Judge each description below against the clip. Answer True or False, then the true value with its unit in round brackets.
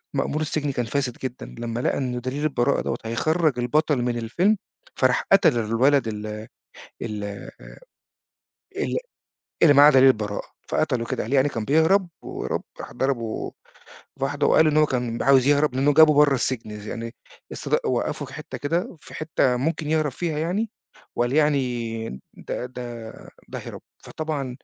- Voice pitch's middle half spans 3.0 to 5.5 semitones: True (4.0 semitones)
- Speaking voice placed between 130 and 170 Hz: True (135 Hz)